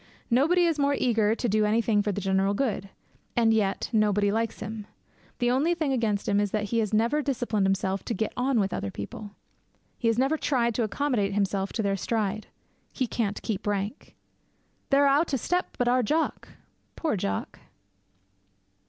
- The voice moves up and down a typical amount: Yes, average, 4.1 semitones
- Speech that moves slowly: No, average, 185 wpm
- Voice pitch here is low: No, high, 220 Hz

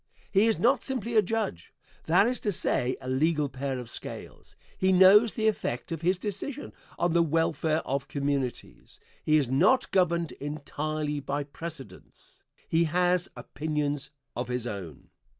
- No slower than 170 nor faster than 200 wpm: No, average, 155 wpm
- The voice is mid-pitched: Yes, medium, 155 Hz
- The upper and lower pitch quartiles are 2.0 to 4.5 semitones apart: No, average, 5.3 semitones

